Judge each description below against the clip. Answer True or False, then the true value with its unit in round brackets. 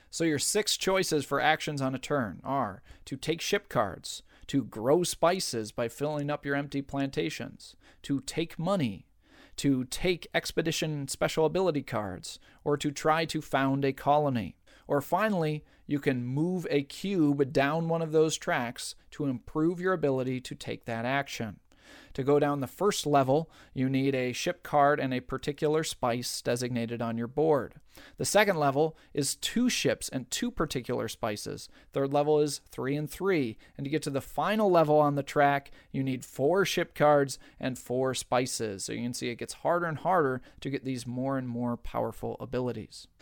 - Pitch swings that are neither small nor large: True (3.3 semitones)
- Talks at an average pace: True (180 wpm)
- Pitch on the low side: False (145 Hz)